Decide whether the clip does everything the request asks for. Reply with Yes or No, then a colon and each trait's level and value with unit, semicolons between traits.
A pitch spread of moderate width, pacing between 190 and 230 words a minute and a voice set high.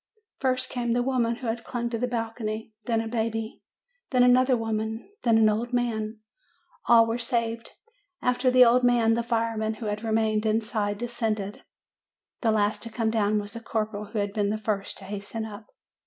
No: narrow, 1.8 semitones; average, 195 wpm; high, 225 Hz